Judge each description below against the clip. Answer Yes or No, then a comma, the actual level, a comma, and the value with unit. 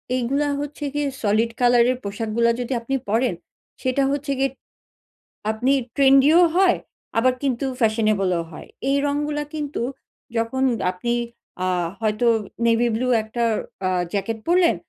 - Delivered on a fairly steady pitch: No, average, 3.9 semitones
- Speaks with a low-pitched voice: No, high, 245 Hz